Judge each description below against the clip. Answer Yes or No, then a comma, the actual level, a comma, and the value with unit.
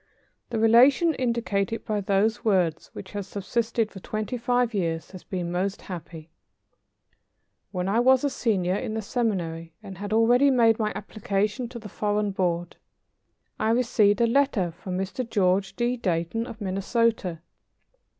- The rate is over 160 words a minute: No, average, 150 wpm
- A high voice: Yes, high, 210 Hz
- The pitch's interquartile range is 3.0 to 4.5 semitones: Yes, average, 3.9 semitones